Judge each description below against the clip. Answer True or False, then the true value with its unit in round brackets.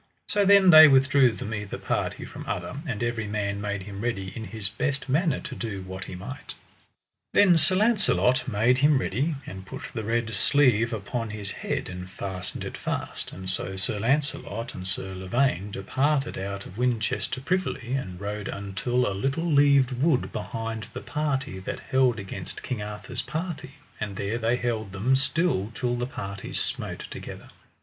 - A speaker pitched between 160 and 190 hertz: False (115 Hz)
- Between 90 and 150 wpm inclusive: False (175 wpm)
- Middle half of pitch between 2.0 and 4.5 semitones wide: False (5.3 semitones)